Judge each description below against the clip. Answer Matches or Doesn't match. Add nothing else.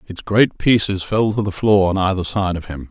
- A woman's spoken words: Doesn't match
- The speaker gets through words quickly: Matches